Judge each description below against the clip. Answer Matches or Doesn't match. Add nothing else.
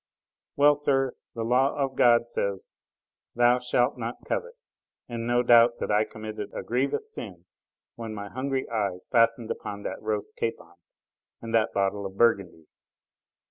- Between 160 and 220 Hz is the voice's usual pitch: Doesn't match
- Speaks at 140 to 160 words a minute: Matches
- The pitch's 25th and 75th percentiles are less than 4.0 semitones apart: Matches